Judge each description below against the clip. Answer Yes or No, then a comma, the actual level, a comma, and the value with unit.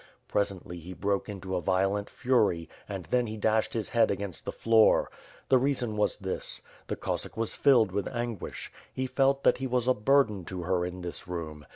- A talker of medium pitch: No, low, 105 Hz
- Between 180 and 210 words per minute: Yes, average, 200 wpm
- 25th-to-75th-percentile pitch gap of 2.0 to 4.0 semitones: No, average, 4.6 semitones